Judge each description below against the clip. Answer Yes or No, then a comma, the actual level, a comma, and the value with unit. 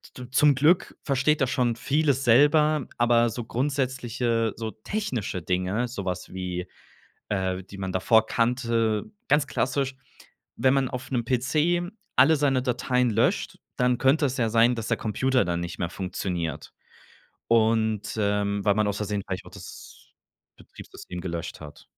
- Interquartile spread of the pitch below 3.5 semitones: No, average, 4.7 semitones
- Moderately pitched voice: No, low, 120 Hz